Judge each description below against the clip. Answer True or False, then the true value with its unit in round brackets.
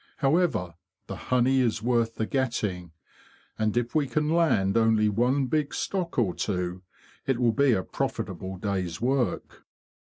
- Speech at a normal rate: True (150 wpm)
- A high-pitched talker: False (120 Hz)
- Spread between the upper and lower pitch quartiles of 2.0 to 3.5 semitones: False (5.2 semitones)